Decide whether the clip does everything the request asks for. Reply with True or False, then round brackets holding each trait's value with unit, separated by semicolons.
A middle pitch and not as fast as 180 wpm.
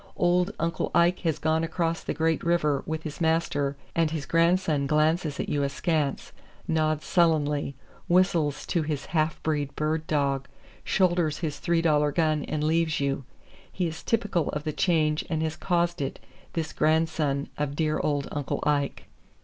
True (155 Hz; 165 wpm)